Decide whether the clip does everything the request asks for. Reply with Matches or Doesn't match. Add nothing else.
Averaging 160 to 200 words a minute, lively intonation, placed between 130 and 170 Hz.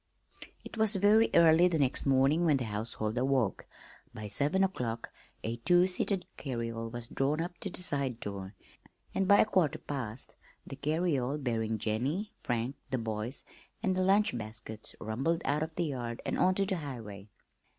Matches